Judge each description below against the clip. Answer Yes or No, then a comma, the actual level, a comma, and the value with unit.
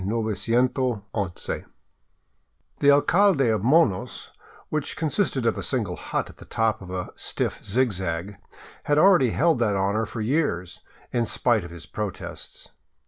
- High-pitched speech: No, low, 115 Hz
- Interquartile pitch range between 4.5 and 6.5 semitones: Yes, wide, 5.6 semitones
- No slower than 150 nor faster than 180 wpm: No, average, 140 wpm